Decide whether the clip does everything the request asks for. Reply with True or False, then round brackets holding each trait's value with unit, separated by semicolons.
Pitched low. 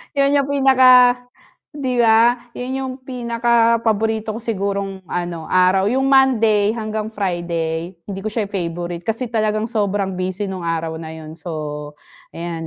False (210 Hz)